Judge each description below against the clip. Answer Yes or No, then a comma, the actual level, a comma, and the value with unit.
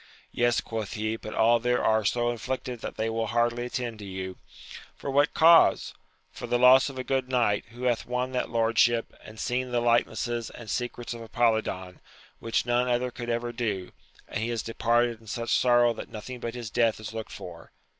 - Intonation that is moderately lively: No, narrow, 1.6 semitones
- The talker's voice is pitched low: Yes, low, 120 Hz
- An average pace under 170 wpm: No, fast, 205 wpm